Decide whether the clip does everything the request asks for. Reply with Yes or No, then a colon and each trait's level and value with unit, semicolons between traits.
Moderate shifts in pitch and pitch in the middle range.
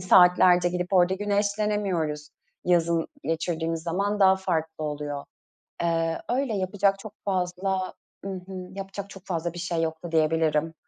Yes: average, 3.0 semitones; medium, 180 Hz